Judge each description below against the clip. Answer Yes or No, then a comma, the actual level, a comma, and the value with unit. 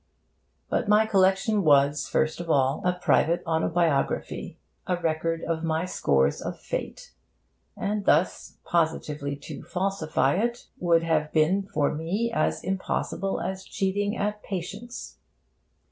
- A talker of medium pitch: Yes, medium, 175 Hz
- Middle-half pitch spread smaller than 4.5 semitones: Yes, average, 3.7 semitones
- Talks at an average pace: No, slow, 130 wpm